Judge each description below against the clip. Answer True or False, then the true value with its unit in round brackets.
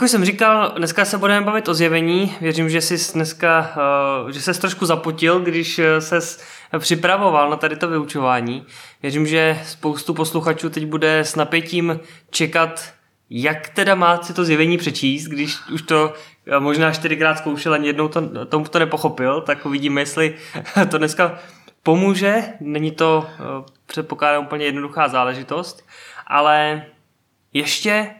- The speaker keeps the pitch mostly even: True (2.2 semitones)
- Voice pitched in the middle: True (160 Hz)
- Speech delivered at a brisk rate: False (140 wpm)